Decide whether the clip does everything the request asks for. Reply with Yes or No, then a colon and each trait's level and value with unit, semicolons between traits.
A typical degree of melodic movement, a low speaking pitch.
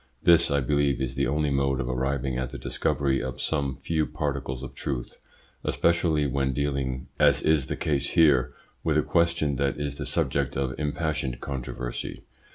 No: narrow, 2.2 semitones; very low, 70 Hz